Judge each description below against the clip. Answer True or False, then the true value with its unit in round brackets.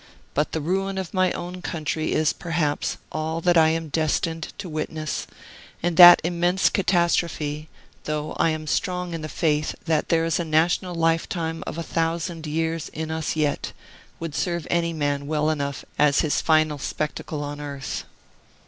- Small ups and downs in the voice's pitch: True (1.9 semitones)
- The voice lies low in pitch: False (160 Hz)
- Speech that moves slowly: False (165 wpm)